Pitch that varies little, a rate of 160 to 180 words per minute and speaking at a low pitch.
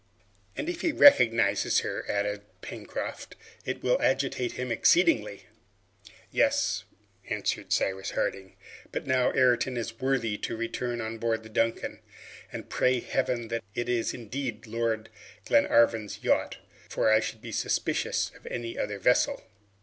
No: narrow, 2.3 semitones; average, 140 wpm; low, 115 Hz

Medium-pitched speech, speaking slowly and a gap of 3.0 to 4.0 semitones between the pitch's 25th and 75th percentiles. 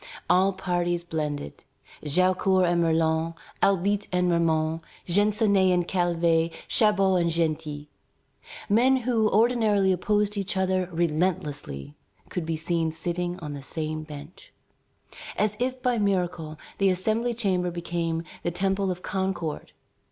Yes: medium, 180 Hz; slow, 125 wpm; average, 3.3 semitones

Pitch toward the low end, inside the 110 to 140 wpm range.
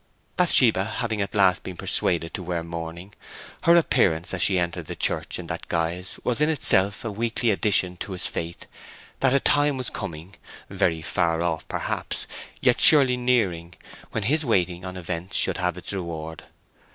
No: very low, 95 Hz; average, 165 wpm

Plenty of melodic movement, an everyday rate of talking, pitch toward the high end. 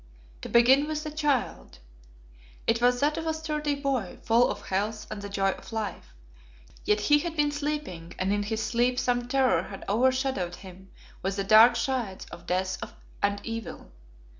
Yes: wide, 5.7 semitones; average, 180 wpm; high, 235 Hz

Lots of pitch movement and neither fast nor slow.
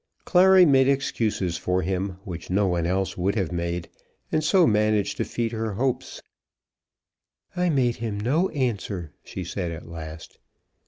Yes: wide, 6.7 semitones; average, 155 wpm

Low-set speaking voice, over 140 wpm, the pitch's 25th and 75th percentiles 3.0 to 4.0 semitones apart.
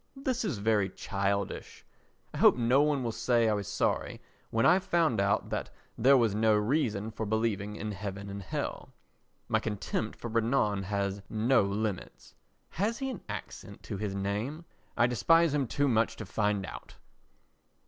No: low, 110 Hz; average, 170 wpm; average, 4.7 semitones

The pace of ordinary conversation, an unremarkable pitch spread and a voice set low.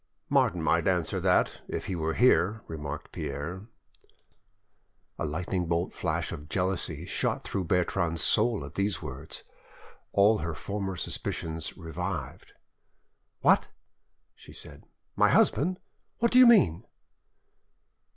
No: slow, 120 wpm; average, 3.6 semitones; very low, 90 Hz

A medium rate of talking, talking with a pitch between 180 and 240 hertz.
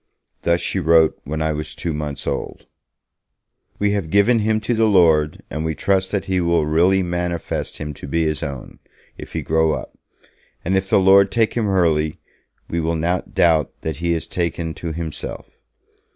No: average, 185 wpm; very low, 85 Hz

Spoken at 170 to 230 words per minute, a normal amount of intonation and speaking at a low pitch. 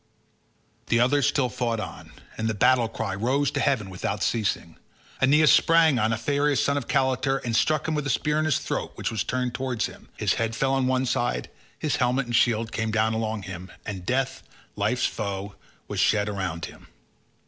Yes: average, 200 wpm; average, 3.6 semitones; low, 120 Hz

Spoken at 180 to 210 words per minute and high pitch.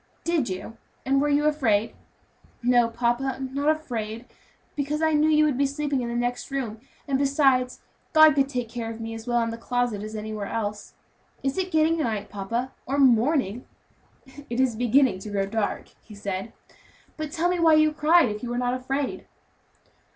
Yes: average, 190 wpm; very high, 250 Hz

